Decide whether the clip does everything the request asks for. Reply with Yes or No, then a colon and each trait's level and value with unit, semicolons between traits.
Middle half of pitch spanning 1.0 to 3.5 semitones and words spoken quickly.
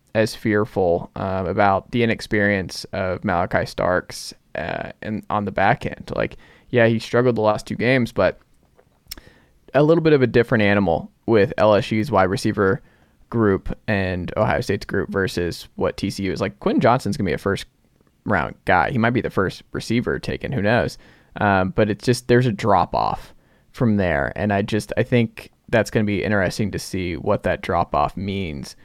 No: average, 3.0 semitones; average, 185 wpm